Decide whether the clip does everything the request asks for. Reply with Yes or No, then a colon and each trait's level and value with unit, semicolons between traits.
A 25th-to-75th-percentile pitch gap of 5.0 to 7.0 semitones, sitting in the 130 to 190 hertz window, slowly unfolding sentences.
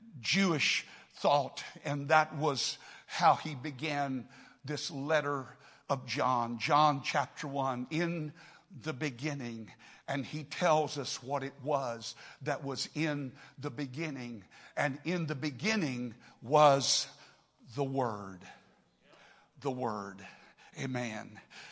No: average, 3.0 semitones; medium, 140 Hz; slow, 110 wpm